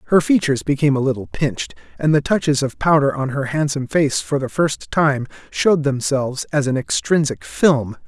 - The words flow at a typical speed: Yes, average, 185 wpm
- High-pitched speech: No, medium, 140 Hz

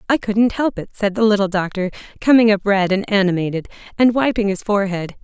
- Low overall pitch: No, high, 205 Hz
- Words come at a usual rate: Yes, average, 195 wpm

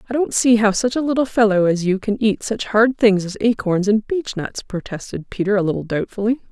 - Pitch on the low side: No, high, 215 Hz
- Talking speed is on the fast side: Yes, fast, 220 wpm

